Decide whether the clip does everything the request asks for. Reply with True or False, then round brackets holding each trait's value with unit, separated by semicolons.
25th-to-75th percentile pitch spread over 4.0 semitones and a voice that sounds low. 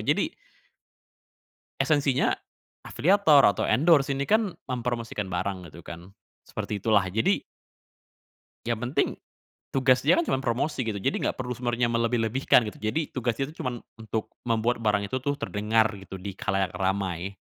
True (4.7 semitones; 115 Hz)